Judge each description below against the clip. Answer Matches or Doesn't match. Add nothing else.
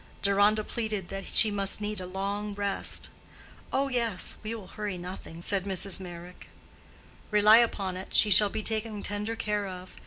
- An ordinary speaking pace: Matches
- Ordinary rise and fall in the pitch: Doesn't match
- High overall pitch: Matches